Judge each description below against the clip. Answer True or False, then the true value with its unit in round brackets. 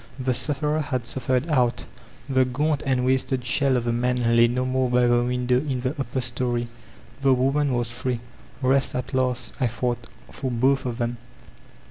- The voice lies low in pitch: True (125 Hz)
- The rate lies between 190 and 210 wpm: False (180 wpm)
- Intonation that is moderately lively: False (1.5 semitones)